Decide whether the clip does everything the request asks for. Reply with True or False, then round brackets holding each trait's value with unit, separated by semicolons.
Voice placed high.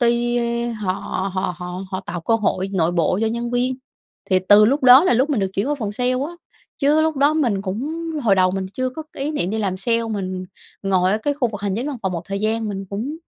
True (220 Hz)